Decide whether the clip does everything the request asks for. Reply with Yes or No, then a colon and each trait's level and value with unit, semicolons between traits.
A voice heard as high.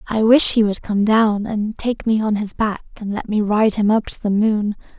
Yes: high, 215 Hz